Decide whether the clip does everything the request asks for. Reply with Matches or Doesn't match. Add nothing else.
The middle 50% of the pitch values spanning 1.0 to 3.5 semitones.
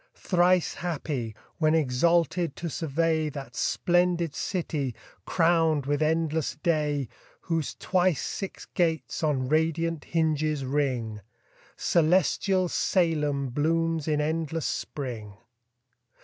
Matches